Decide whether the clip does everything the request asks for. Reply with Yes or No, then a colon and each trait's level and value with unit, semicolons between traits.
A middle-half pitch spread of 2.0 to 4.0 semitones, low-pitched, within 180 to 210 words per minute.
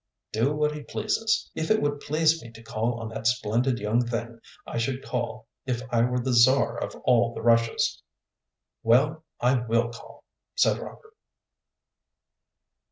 No: average, 3.4 semitones; low, 120 Hz; average, 160 wpm